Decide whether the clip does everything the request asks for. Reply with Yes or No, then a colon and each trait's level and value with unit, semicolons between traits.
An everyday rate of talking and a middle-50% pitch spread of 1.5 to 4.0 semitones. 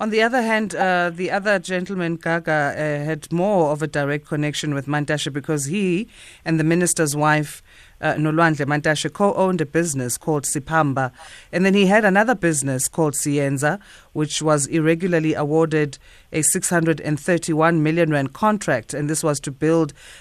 Yes: average, 165 wpm; average, 2.7 semitones